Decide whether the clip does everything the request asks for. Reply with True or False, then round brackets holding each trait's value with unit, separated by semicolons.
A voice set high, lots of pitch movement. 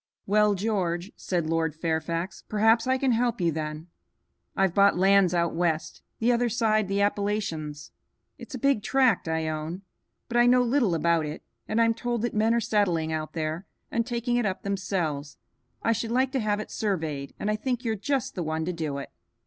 True (200 Hz; 6.0 semitones)